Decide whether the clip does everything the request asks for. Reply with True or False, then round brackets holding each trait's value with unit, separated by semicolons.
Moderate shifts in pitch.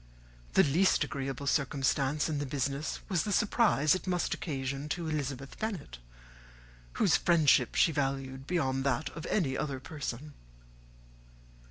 True (3.2 semitones)